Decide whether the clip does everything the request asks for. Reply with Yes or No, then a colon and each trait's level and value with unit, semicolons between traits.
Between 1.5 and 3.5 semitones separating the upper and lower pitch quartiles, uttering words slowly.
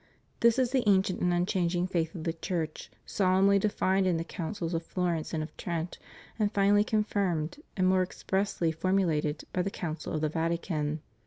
No: average, 3.1 semitones; average, 175 wpm